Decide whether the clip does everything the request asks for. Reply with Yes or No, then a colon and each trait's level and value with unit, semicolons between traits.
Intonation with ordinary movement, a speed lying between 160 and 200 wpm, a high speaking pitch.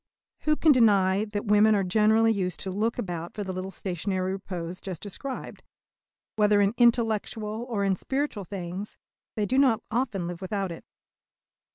Yes: average, 3.0 semitones; average, 165 wpm; high, 205 Hz